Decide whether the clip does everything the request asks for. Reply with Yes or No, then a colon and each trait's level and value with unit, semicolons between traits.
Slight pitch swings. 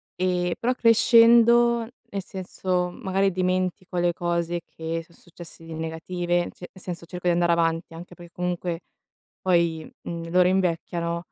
Yes: narrow, 1.6 semitones